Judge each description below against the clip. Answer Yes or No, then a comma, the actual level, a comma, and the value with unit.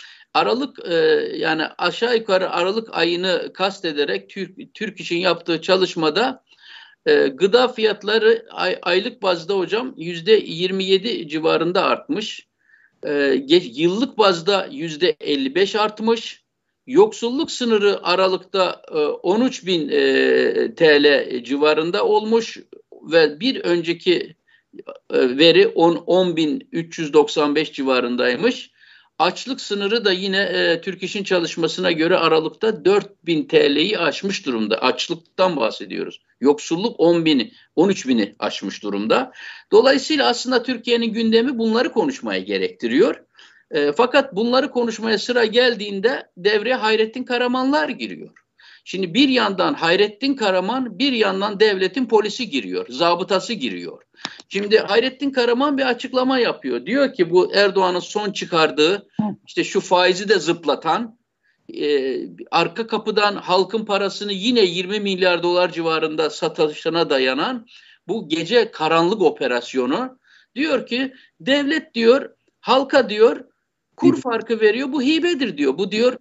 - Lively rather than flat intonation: Yes, wide, 6.6 semitones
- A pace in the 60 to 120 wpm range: Yes, average, 115 wpm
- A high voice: Yes, high, 215 Hz